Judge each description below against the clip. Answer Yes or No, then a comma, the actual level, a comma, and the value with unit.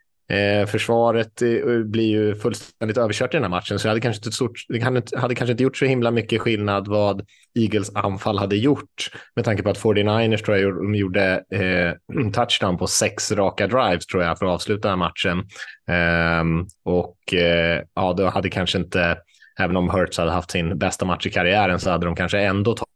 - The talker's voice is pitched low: Yes, low, 100 Hz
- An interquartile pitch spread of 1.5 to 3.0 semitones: No, average, 3.8 semitones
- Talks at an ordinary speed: No, fast, 210 wpm